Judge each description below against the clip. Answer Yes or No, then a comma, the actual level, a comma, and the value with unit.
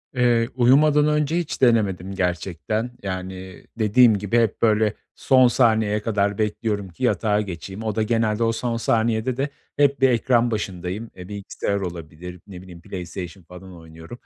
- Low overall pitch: Yes, low, 105 Hz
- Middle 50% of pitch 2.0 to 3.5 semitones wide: No, average, 4.2 semitones